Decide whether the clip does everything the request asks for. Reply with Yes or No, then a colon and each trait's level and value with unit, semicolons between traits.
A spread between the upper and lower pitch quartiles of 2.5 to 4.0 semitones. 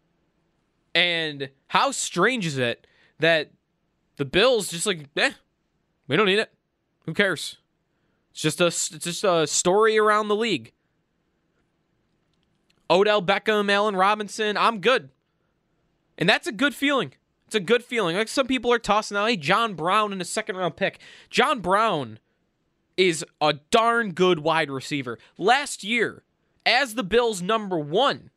No: average, 4.5 semitones